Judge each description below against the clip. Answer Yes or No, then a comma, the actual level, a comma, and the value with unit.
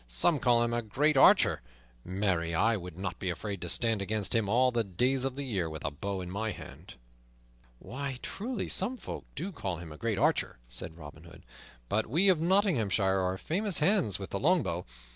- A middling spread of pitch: No, wide, 7.1 semitones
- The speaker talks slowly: No, average, 200 wpm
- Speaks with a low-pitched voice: Yes, low, 110 Hz